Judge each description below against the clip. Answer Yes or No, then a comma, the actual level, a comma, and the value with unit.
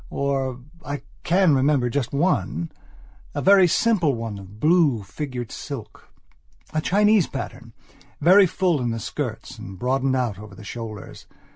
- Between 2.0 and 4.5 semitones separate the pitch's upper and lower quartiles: No, wide, 5.5 semitones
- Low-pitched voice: Yes, low, 130 Hz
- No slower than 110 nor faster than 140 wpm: Yes, slow, 135 wpm